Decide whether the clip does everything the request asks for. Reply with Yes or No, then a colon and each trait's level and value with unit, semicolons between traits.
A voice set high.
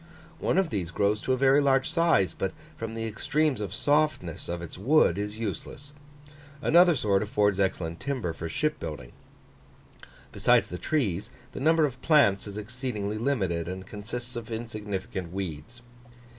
No: low, 110 Hz